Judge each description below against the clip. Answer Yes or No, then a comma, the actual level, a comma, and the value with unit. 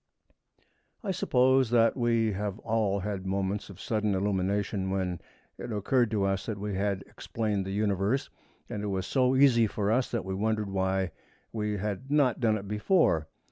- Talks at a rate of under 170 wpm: No, average, 175 wpm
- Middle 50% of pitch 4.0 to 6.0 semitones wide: No, average, 2.9 semitones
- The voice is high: No, low, 105 Hz